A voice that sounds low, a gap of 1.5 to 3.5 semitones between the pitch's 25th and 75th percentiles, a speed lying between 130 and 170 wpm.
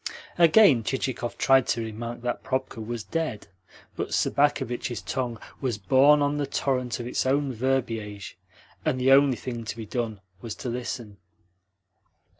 Yes: low, 125 Hz; average, 2.7 semitones; average, 150 wpm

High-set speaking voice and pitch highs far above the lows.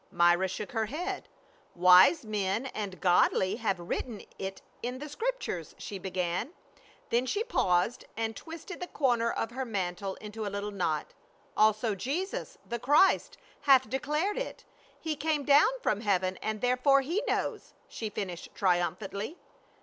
Yes: high, 220 Hz; wide, 6.8 semitones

